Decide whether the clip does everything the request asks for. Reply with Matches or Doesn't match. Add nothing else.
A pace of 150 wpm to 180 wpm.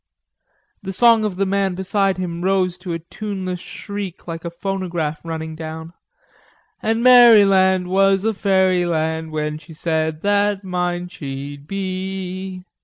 Doesn't match